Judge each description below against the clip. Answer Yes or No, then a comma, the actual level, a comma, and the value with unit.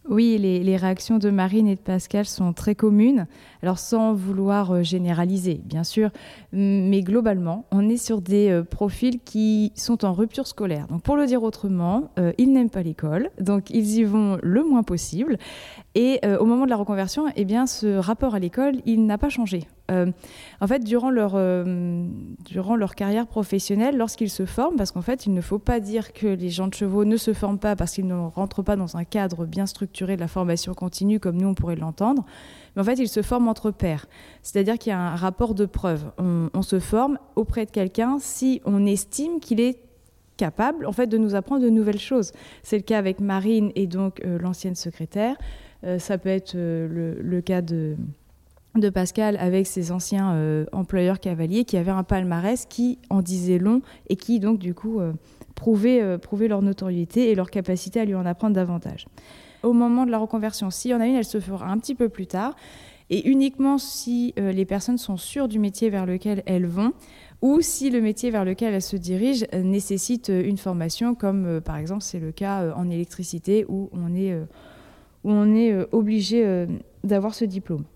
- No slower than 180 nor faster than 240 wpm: Yes, average, 210 wpm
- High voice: Yes, high, 200 Hz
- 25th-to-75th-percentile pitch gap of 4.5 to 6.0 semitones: No, average, 3.6 semitones